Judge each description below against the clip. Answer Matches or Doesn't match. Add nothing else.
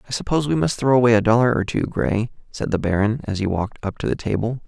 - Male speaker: Matches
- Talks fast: Matches